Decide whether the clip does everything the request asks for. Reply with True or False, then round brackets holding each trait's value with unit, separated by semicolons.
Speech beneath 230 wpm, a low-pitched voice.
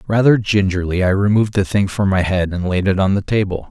False (245 wpm; 95 Hz)